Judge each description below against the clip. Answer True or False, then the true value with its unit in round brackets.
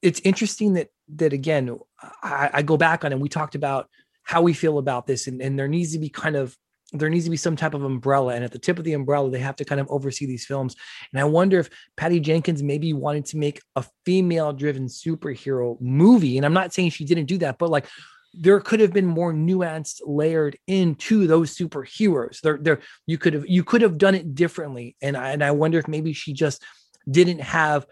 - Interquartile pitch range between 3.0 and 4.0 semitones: True (3.5 semitones)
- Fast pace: True (230 wpm)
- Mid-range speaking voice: True (155 Hz)